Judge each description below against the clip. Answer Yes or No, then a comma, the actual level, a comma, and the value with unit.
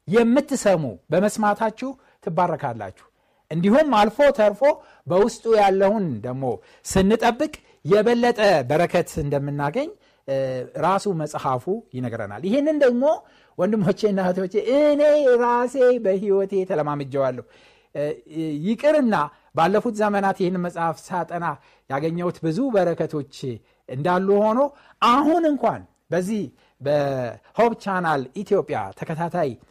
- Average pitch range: No, wide, 7.3 semitones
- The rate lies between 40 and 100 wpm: Yes, average, 85 wpm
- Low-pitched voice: No, high, 190 Hz